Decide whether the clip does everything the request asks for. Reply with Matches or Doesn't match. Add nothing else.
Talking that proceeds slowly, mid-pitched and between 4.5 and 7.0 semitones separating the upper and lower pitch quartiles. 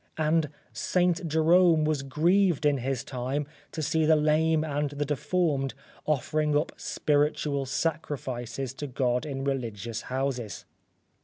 Doesn't match